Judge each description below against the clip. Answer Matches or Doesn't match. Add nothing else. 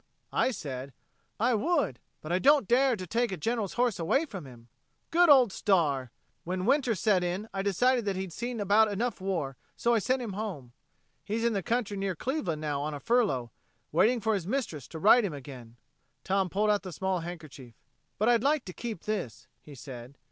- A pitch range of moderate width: Doesn't match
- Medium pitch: Doesn't match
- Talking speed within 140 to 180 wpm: Doesn't match